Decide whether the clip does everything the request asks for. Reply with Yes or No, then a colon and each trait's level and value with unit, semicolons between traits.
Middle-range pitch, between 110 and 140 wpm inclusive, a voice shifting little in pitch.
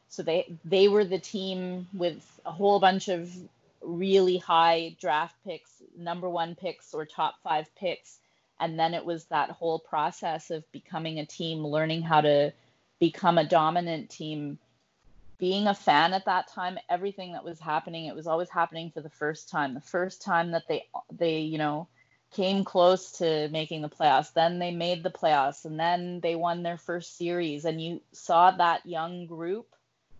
No: medium, 170 Hz; average, 180 wpm; narrow, 2.2 semitones